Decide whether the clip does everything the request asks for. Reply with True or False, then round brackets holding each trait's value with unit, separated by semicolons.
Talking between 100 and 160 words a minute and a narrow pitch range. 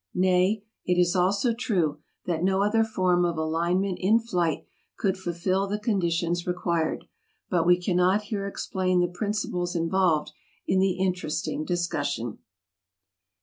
True (135 wpm; 2.2 semitones)